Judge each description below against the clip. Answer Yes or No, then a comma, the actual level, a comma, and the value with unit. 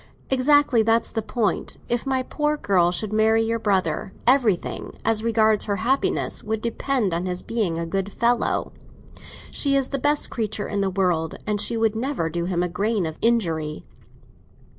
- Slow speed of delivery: No, average, 165 wpm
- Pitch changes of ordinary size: Yes, average, 4.2 semitones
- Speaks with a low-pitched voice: No, high, 220 Hz